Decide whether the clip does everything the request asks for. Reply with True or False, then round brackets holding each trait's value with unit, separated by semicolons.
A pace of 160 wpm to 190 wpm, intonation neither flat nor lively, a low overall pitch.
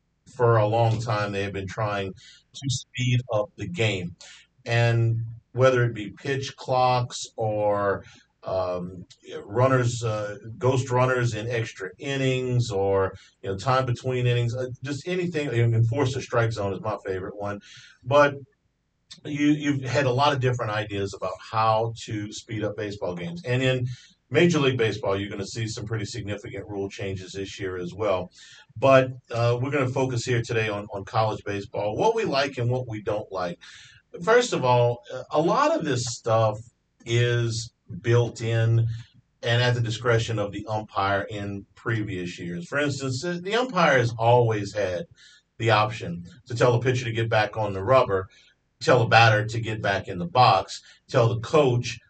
True (175 wpm; 3.6 semitones; 115 Hz)